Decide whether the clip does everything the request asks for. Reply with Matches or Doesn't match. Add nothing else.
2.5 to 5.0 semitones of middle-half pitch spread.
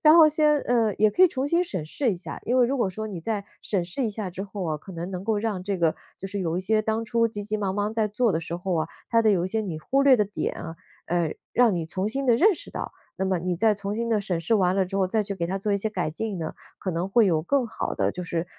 Matches